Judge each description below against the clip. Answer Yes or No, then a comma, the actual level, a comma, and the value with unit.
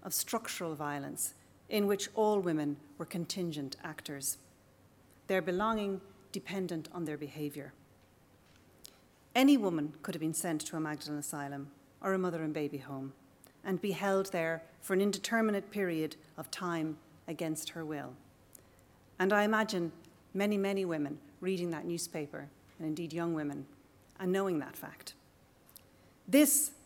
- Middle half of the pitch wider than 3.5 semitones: Yes, average, 4.7 semitones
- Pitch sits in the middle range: Yes, medium, 165 Hz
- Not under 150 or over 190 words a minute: No, average, 140 wpm